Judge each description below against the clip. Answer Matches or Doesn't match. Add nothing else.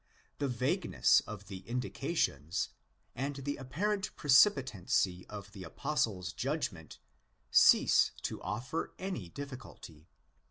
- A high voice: Doesn't match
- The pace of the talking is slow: Matches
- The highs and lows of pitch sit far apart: Matches